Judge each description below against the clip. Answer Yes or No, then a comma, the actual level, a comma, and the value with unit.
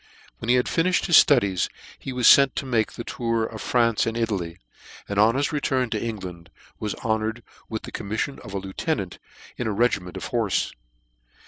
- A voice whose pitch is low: Yes, low, 115 Hz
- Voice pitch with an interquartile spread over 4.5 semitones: No, average, 3.4 semitones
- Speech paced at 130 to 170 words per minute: No, average, 195 wpm